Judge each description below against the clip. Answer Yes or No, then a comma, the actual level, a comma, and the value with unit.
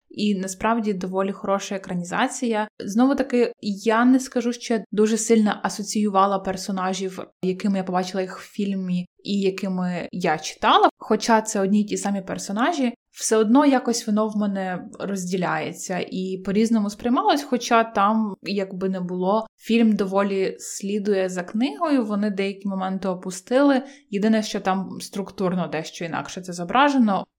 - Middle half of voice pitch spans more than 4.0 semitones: No, average, 3.3 semitones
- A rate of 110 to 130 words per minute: No, average, 140 wpm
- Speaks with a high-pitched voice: Yes, high, 205 Hz